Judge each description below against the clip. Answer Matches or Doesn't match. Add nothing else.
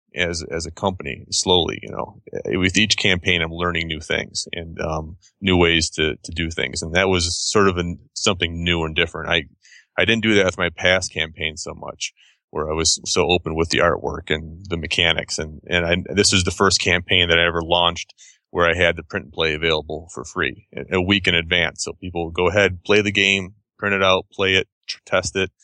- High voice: Doesn't match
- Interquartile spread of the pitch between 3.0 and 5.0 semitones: Doesn't match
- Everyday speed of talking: Doesn't match